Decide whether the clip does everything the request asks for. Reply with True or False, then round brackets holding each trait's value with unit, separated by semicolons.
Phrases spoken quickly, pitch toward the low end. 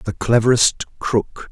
False (120 wpm; 110 Hz)